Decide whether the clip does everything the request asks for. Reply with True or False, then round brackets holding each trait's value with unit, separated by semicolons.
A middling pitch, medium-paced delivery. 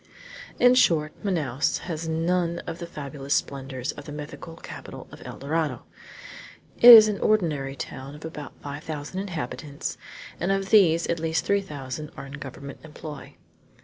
True (155 Hz; 160 wpm)